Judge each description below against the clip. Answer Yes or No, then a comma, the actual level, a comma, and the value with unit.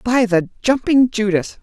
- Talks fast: No, average, 150 wpm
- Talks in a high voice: Yes, high, 225 Hz